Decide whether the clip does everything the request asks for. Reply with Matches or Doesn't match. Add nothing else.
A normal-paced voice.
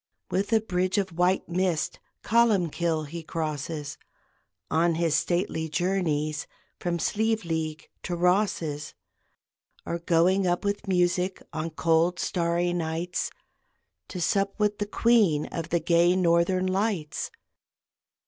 Doesn't match